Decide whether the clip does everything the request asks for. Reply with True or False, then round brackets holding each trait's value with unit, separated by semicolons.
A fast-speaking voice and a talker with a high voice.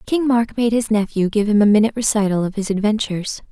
True (220 wpm; 215 Hz)